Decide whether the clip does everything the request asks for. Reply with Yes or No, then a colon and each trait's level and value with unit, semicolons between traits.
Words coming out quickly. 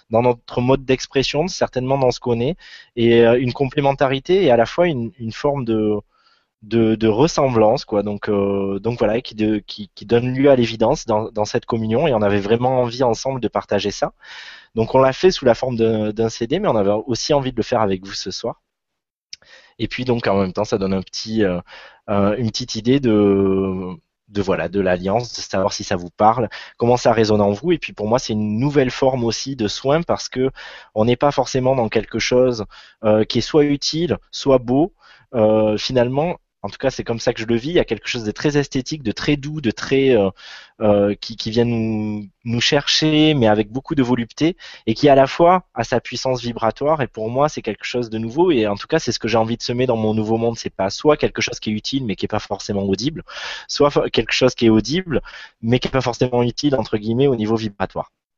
Yes: fast, 235 wpm